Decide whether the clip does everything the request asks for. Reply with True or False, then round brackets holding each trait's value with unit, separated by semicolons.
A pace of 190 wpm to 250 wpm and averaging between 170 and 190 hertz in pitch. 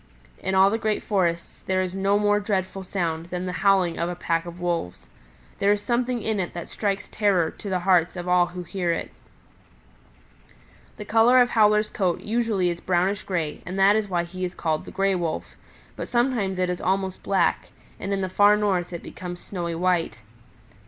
True (200 wpm; 185 Hz)